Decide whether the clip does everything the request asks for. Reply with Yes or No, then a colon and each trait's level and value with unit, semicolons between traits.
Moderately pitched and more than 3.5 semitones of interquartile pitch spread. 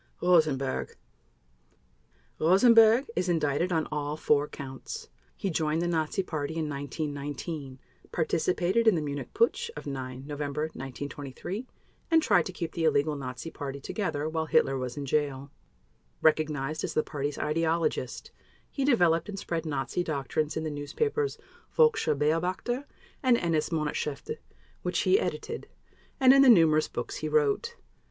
Yes: medium, 155 Hz; average, 4.2 semitones